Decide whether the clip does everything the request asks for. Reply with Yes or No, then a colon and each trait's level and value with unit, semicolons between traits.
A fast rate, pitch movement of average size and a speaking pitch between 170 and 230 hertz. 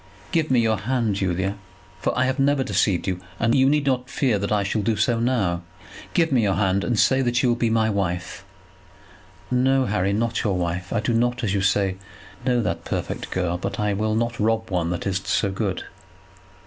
No: fast, 210 wpm; average, 4.1 semitones; low, 110 Hz